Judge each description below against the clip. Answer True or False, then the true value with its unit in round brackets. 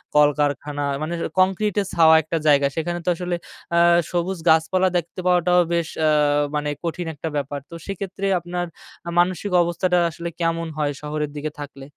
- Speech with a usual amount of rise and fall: True (3.0 semitones)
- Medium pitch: True (165 Hz)